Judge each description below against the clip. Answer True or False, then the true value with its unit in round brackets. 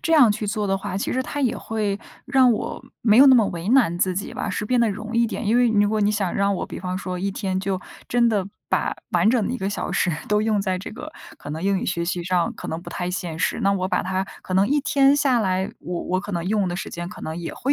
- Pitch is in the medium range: False (200 Hz)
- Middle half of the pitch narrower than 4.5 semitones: True (3.8 semitones)